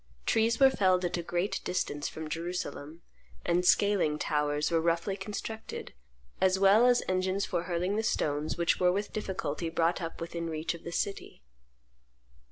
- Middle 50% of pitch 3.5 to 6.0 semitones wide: No, average, 3.0 semitones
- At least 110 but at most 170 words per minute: Yes, average, 165 wpm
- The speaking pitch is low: No, medium, 175 Hz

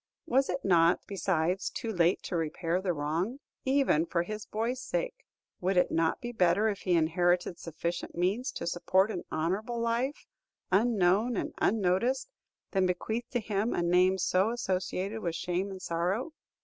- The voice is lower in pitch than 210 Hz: Yes, high, 190 Hz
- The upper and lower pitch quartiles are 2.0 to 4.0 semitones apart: No, average, 4.4 semitones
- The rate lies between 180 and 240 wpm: No, average, 160 wpm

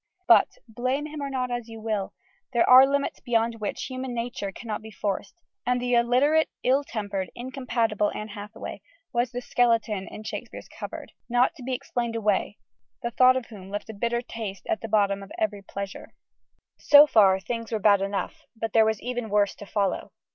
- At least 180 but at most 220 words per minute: Yes, average, 190 wpm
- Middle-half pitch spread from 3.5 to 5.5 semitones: No, average, 3.1 semitones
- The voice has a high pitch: Yes, high, 230 Hz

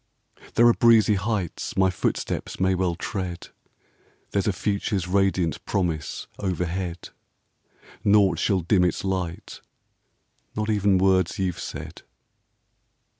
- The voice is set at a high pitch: No, very low, 95 Hz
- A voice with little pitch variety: Yes, narrow, 2.1 semitones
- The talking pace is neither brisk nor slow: No, slow, 125 wpm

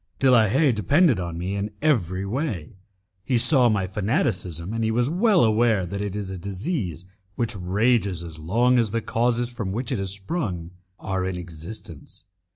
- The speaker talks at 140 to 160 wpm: No, average, 180 wpm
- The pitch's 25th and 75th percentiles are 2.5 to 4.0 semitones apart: No, average, 4.8 semitones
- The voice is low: Yes, low, 105 Hz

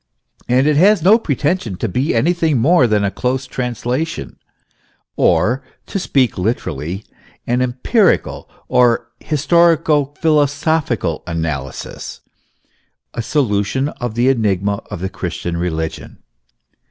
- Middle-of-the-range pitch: No, low, 125 Hz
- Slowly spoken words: Yes, slow, 115 wpm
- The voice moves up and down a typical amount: No, wide, 6.9 semitones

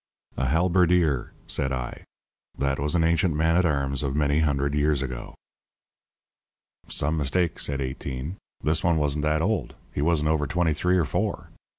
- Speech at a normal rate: Yes, average, 165 wpm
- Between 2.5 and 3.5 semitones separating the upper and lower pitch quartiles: Yes, average, 3.1 semitones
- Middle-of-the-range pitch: No, very low, 75 Hz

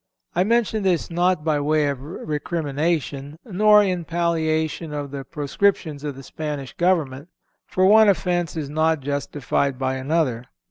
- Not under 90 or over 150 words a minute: Yes, average, 145 wpm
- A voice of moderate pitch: Yes, medium, 155 Hz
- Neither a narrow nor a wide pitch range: Yes, average, 3.6 semitones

